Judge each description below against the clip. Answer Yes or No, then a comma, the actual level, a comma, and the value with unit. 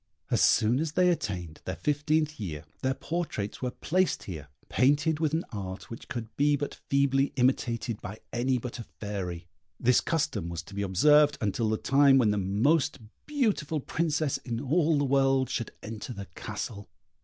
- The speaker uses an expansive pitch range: Yes, wide, 6.2 semitones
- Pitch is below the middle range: Yes, low, 130 Hz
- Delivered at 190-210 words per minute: No, average, 175 wpm